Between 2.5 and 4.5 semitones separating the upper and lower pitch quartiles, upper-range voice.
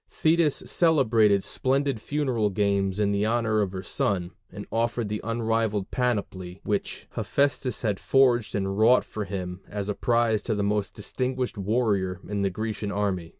No: average, 3.2 semitones; low, 105 Hz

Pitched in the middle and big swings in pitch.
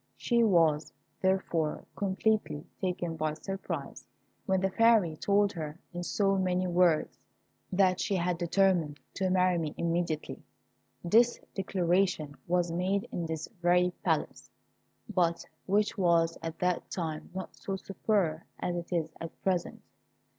No: medium, 180 Hz; narrow, 2.6 semitones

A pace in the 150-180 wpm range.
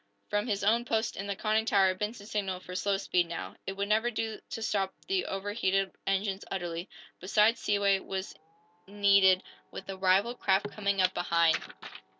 Yes: average, 170 wpm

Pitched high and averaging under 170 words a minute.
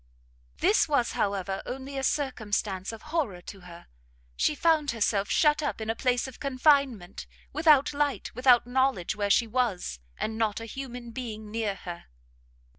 Yes: high, 240 Hz; average, 160 wpm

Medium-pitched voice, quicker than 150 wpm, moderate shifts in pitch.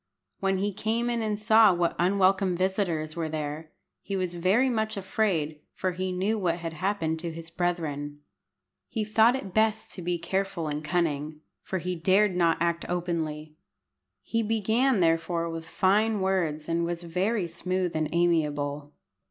Yes: medium, 180 Hz; average, 160 wpm; average, 3.5 semitones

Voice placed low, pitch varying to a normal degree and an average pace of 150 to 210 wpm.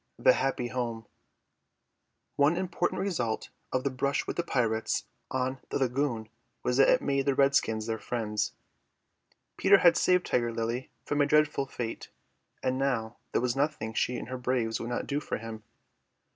Yes: low, 130 Hz; average, 3.5 semitones; average, 160 wpm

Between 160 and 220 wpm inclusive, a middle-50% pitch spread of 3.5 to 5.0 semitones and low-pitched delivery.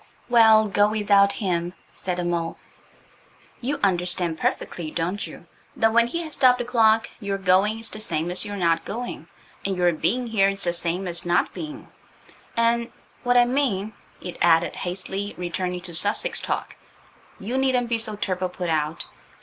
No: average, 170 wpm; average, 4.7 semitones; high, 200 Hz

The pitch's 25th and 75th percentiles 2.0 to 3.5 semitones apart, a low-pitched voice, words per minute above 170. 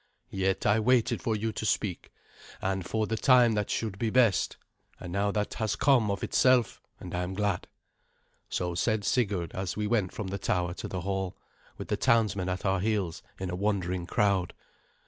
Yes: average, 3.0 semitones; low, 100 Hz; average, 190 wpm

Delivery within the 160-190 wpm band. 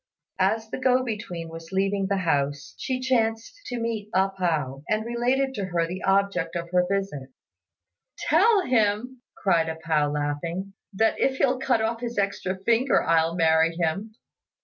Yes: average, 165 wpm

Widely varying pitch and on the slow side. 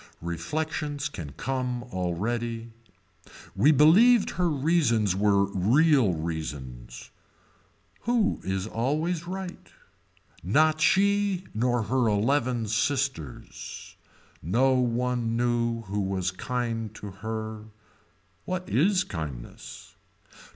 Yes: wide, 7.2 semitones; slow, 95 wpm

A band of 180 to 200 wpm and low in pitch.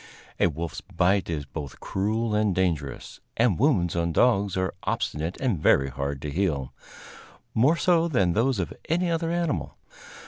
No: average, 160 wpm; very low, 95 Hz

